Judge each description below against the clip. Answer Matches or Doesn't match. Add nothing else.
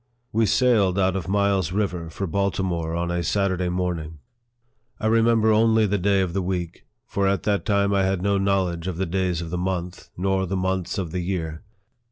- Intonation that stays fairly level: Matches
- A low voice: Matches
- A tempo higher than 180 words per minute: Matches